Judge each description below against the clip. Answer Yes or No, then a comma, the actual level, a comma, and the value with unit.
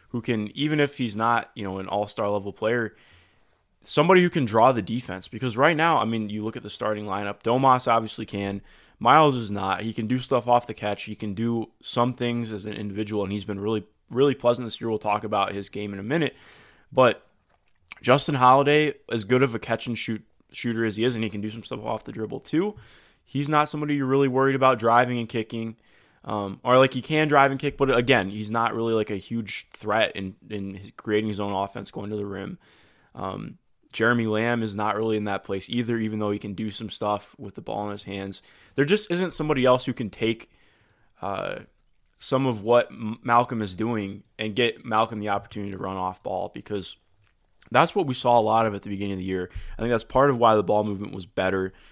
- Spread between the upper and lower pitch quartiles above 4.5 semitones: No, average, 3.2 semitones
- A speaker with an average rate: No, fast, 230 wpm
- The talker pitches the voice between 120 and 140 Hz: No, low, 110 Hz